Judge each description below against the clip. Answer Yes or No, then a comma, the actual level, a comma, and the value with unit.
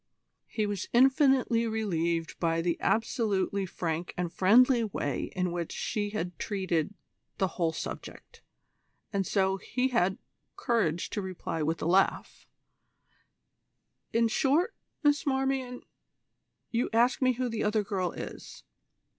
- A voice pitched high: Yes, high, 205 Hz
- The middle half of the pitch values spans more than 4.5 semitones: Yes, average, 5.2 semitones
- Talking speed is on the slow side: Yes, slow, 130 wpm